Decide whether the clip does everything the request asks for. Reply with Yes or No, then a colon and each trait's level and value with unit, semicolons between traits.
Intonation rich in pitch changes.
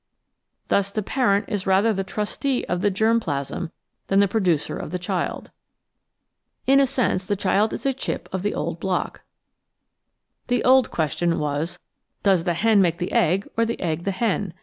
No: average, 4.0 semitones